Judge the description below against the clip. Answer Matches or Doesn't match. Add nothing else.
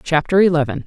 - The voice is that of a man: Doesn't match